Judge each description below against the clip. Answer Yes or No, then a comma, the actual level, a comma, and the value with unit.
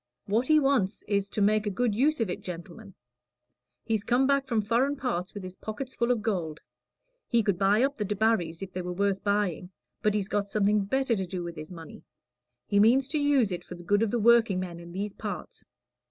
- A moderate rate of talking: No, fast, 220 wpm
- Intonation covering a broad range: No, average, 4.1 semitones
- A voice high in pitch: Yes, high, 205 Hz